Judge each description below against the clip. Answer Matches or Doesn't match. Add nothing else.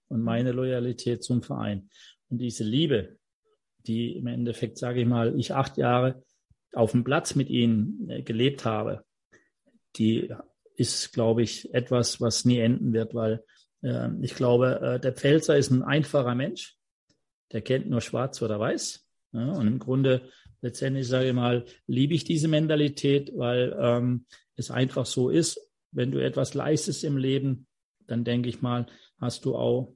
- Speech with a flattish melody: Matches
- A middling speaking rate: Matches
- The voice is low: Matches